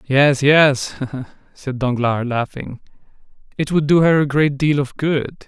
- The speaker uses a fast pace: No, average, 155 wpm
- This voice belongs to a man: Yes, male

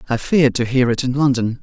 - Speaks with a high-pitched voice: No, low, 125 Hz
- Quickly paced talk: Yes, fast, 260 wpm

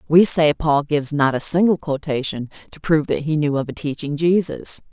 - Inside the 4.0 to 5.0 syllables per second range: No, 5.4 syllables/s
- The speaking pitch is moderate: Yes, medium, 150 Hz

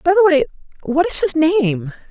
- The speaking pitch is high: Yes, very high, 300 Hz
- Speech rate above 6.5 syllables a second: No, 5.0 syllables/s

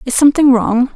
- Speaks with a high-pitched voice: Yes, very high, 260 Hz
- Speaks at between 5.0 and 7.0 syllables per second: Yes, 6.1 syllables/s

